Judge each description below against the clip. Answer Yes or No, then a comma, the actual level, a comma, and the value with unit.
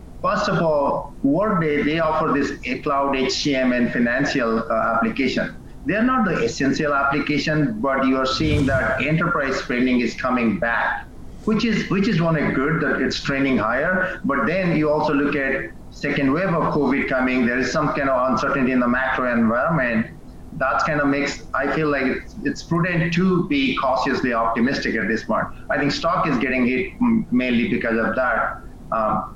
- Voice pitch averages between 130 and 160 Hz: Yes, medium, 140 Hz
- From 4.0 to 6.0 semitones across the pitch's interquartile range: Yes, average, 4.3 semitones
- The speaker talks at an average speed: Yes, average, 180 wpm